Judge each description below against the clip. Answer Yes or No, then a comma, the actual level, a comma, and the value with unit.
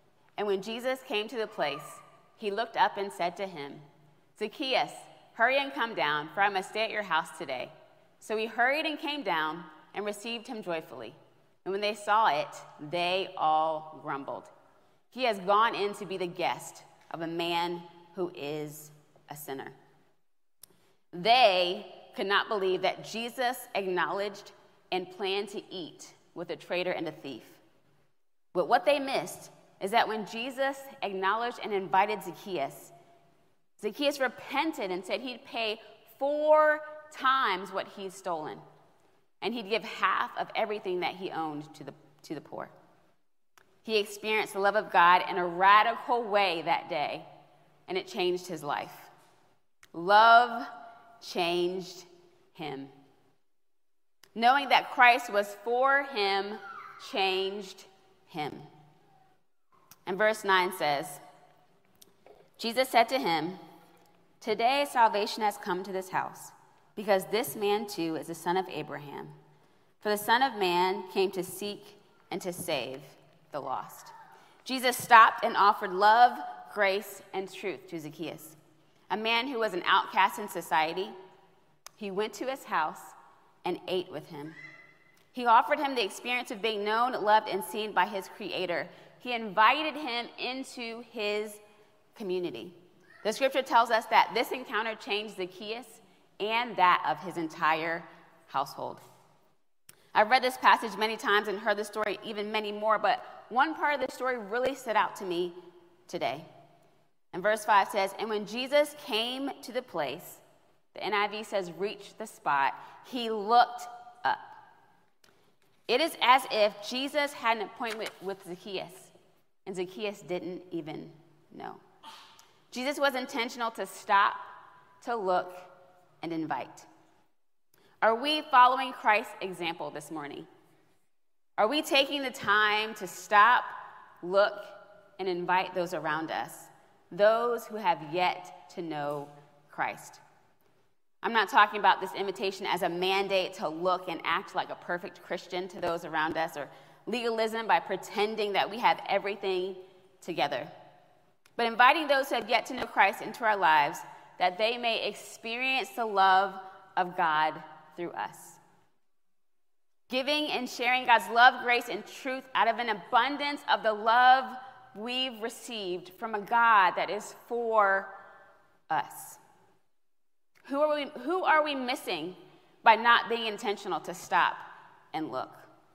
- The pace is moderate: Yes, average, 145 wpm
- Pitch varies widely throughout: No, average, 4.7 semitones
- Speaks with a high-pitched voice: Yes, high, 205 Hz